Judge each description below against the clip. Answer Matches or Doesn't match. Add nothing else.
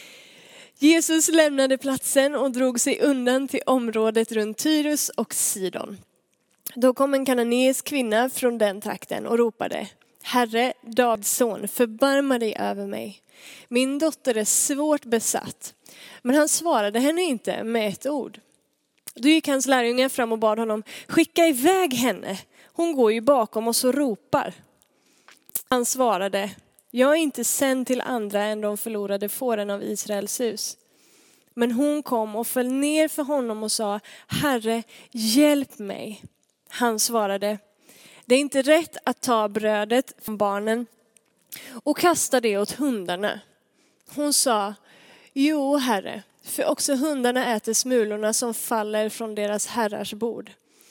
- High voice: Matches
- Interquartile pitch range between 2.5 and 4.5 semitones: Matches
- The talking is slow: Doesn't match